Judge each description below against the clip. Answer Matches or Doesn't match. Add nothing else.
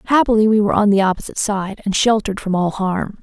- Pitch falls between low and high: Doesn't match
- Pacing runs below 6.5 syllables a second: Doesn't match